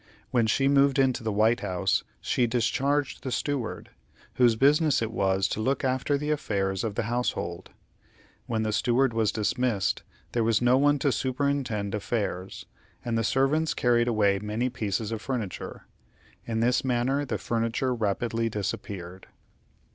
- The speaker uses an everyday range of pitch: Yes, average, 3.7 semitones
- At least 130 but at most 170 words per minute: Yes, average, 155 wpm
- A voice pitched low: Yes, low, 115 Hz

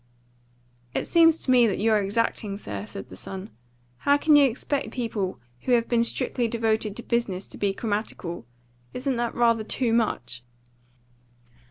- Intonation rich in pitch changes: No, average, 3.4 semitones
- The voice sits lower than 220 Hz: No, high, 225 Hz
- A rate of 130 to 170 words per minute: Yes, average, 160 wpm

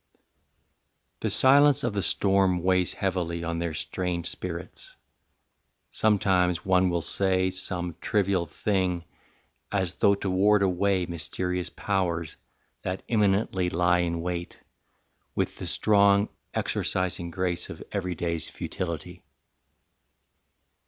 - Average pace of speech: No, slow, 110 wpm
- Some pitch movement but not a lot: No, narrow, 2.1 semitones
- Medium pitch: No, very low, 90 Hz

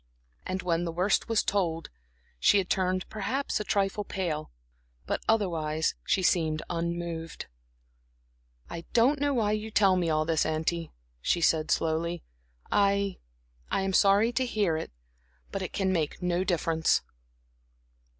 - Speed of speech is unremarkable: Yes, average, 145 wpm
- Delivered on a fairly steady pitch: No, average, 3.5 semitones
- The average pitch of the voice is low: No, medium, 180 Hz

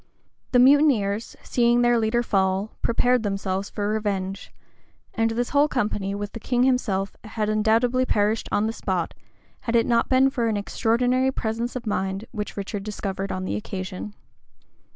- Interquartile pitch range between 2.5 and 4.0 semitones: Yes, average, 3.2 semitones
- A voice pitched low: No, high, 220 Hz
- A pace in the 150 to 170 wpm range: Yes, average, 160 wpm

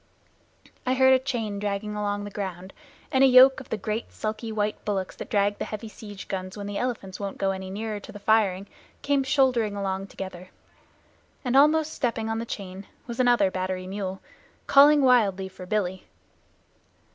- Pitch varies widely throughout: No, average, 4.0 semitones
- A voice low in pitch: No, high, 210 Hz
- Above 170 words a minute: Yes, average, 180 wpm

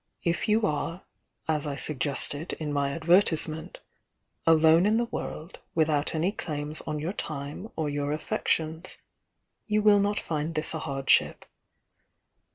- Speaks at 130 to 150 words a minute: Yes, average, 145 wpm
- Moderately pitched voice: Yes, medium, 160 Hz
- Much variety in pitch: No, average, 2.9 semitones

